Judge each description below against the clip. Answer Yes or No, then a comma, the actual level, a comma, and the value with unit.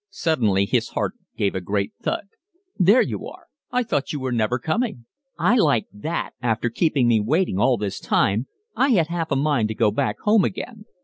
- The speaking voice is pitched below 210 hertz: Yes, low, 135 Hz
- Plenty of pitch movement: Yes, wide, 8.6 semitones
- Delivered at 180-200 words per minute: Yes, average, 195 wpm